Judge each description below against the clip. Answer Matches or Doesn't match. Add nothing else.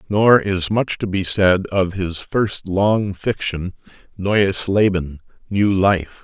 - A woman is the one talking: Doesn't match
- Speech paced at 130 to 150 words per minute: Matches